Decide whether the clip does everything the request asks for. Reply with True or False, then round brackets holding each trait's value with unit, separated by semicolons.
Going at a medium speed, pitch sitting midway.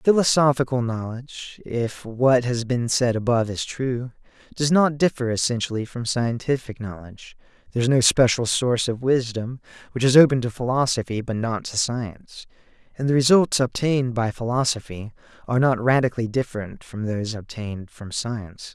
False (155 wpm; 120 Hz)